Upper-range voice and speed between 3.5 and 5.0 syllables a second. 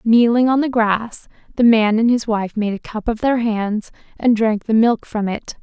Yes: high, 225 Hz; 4.5 syllables/s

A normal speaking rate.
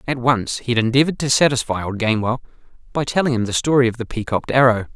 No: fast, 220 wpm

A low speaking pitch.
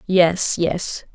No: medium, 175 Hz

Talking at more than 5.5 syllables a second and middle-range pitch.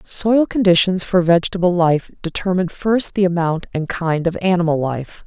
No: 5.0 syllables/s; medium, 180 Hz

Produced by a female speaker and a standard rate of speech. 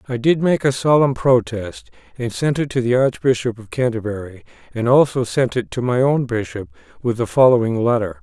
No: male; average, 190 wpm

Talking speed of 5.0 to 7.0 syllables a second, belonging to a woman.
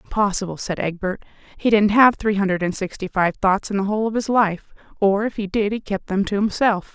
Yes: 5.6 syllables/s; female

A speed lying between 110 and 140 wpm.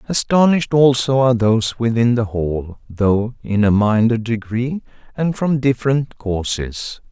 Yes: slow, 135 wpm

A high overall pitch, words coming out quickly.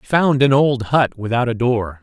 No: low, 125 Hz; fast, 235 wpm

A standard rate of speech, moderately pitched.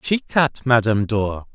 No: average, 155 wpm; low, 120 Hz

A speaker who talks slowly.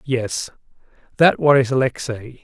Yes: slow, 100 wpm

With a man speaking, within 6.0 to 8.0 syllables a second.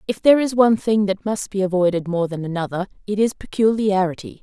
No: female; 6.1 syllables/s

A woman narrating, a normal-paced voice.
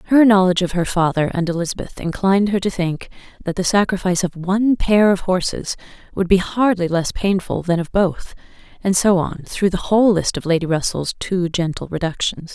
Yes: female; average, 190 wpm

